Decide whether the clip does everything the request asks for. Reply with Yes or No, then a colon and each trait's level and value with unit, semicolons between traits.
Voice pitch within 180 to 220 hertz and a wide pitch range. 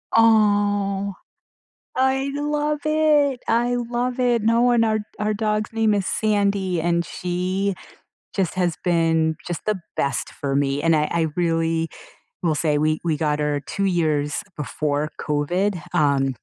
Yes: medium, 185 Hz; wide, 5.9 semitones